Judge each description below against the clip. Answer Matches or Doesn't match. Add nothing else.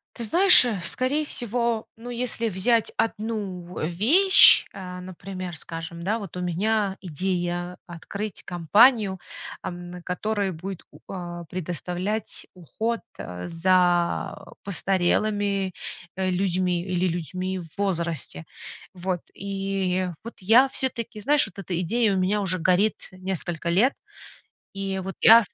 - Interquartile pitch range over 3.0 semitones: Matches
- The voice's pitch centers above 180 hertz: Matches